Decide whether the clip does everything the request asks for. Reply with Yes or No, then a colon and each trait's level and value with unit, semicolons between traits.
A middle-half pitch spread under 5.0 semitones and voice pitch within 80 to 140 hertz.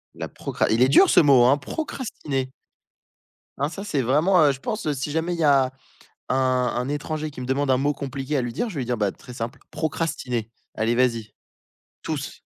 Yes: average, 3.6 semitones; low, 135 Hz